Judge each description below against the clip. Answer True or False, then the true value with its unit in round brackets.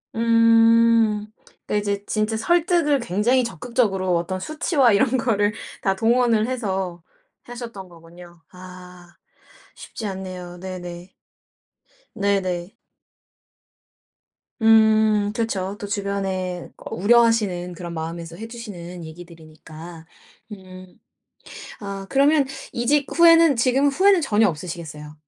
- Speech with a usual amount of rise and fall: True (4.5 semitones)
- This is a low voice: False (205 Hz)